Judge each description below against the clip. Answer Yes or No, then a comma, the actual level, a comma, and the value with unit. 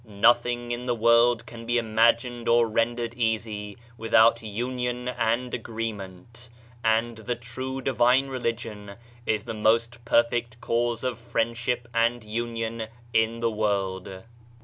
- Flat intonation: Yes, narrow, 1.3 semitones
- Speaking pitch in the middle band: No, low, 115 Hz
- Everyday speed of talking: No, slow, 125 wpm